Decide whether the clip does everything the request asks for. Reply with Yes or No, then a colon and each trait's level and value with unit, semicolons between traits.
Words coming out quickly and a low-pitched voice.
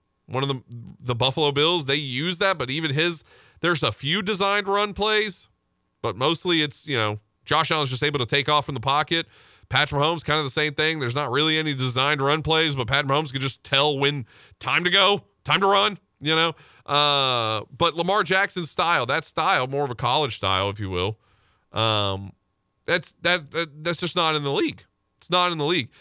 No: fast, 210 wpm; medium, 145 Hz